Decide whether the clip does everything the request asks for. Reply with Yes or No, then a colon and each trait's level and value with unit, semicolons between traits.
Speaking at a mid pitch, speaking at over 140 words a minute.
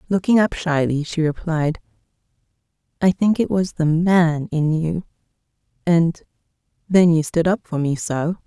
No: medium, 165 Hz; slow, 135 wpm